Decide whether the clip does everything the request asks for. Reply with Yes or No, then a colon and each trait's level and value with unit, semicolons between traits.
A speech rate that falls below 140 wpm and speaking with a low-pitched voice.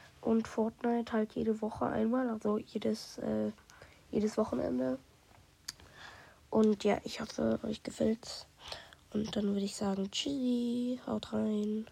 No: slow, 125 wpm; high, 220 Hz